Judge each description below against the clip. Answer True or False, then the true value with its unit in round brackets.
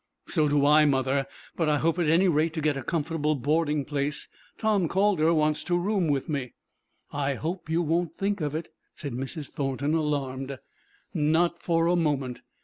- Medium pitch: True (155 Hz)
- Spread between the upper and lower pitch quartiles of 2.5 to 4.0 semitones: True (2.9 semitones)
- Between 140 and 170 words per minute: False (180 wpm)